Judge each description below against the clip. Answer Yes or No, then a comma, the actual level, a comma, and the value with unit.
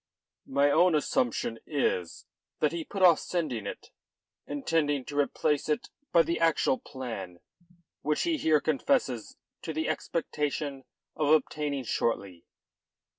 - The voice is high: No, medium, 145 Hz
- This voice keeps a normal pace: No, slow, 125 wpm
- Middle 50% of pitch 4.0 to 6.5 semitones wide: No, average, 3.6 semitones